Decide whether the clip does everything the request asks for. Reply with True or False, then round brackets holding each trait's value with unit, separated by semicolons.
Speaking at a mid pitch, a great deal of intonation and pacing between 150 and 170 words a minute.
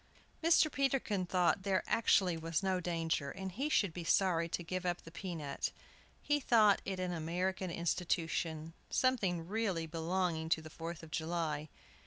False (175 Hz; 2.7 semitones; 165 wpm)